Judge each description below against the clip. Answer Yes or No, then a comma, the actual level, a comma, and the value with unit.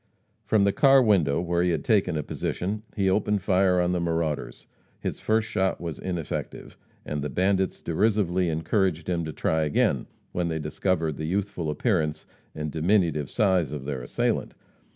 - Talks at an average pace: Yes, average, 170 wpm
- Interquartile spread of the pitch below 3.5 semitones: No, average, 3.8 semitones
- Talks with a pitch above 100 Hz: No, very low, 90 Hz